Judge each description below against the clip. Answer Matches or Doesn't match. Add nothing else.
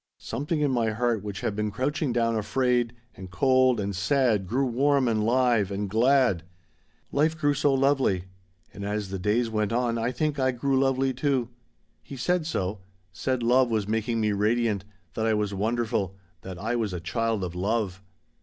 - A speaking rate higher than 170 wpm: Matches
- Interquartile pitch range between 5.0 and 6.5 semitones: Doesn't match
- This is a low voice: Matches